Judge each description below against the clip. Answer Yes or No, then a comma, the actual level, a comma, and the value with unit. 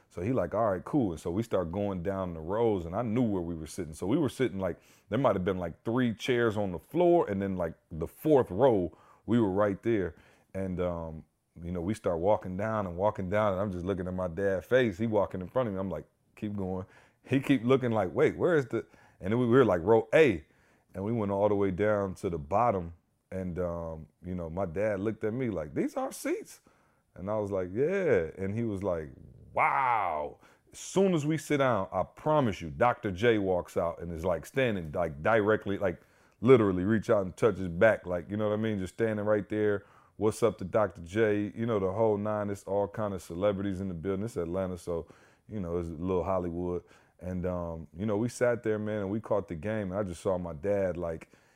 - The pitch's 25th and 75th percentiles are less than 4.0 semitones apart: Yes, average, 3.4 semitones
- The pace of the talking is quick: Yes, fast, 240 wpm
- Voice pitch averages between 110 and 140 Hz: No, low, 100 Hz